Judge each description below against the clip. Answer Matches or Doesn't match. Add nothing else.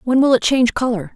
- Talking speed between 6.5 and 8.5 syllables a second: Matches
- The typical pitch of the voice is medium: Doesn't match